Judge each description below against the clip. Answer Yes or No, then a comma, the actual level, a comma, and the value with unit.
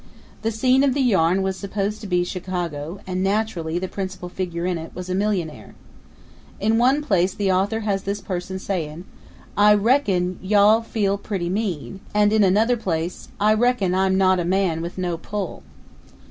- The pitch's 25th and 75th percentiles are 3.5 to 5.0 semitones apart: No, average, 2.8 semitones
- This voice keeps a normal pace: Yes, average, 175 wpm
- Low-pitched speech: No, high, 190 Hz